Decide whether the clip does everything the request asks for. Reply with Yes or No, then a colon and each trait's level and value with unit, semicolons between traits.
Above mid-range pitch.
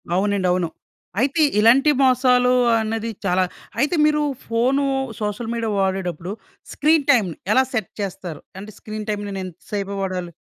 Yes: high, 215 Hz